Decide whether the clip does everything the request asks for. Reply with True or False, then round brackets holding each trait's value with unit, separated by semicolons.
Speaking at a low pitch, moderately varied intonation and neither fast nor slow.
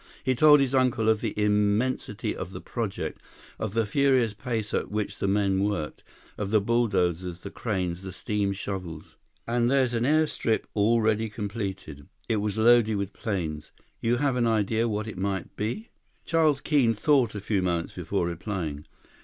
True (105 Hz; 3.5 semitones; 170 wpm)